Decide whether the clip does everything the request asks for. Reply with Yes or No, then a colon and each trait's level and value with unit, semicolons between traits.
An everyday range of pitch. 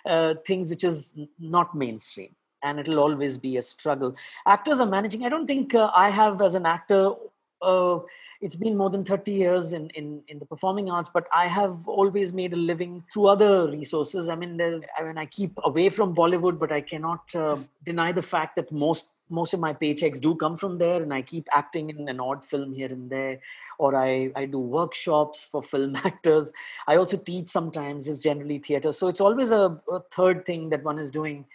Yes: average, 3.8 semitones